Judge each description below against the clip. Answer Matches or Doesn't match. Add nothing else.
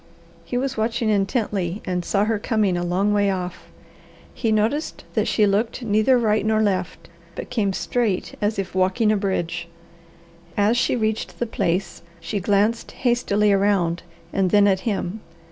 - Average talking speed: Matches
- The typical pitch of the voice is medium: Doesn't match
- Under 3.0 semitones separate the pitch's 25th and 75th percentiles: Matches